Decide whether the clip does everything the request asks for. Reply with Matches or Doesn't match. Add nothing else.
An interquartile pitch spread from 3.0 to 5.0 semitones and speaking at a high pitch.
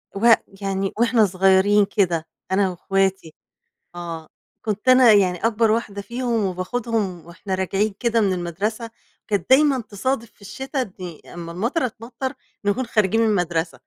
Matches